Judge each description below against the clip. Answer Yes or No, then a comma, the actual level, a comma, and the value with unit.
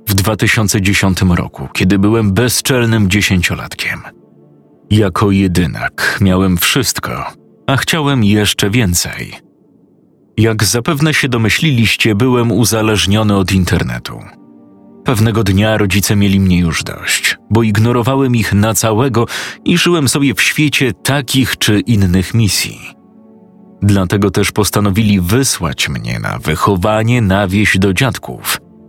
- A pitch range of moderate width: Yes, average, 3.7 semitones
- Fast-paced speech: No, average, 115 wpm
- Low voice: Yes, low, 105 Hz